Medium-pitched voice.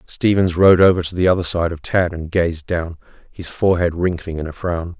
No: very low, 85 Hz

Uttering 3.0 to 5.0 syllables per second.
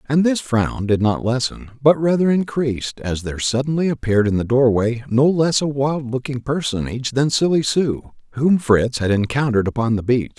No: 5.3 syllables/s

